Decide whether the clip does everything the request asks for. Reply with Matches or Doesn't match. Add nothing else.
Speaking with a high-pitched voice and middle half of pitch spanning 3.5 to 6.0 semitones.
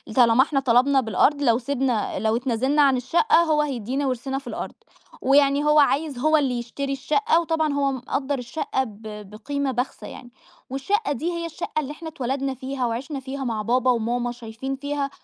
Doesn't match